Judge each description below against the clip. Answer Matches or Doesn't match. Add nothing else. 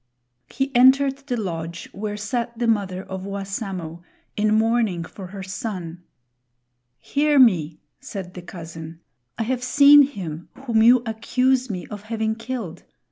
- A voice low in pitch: Doesn't match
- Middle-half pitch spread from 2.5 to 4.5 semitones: Doesn't match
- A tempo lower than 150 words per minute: Matches